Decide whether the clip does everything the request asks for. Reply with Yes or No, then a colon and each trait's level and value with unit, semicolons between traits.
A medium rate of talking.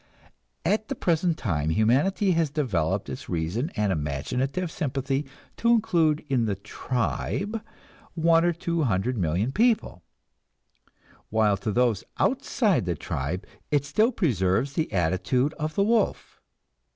No: slow, 130 wpm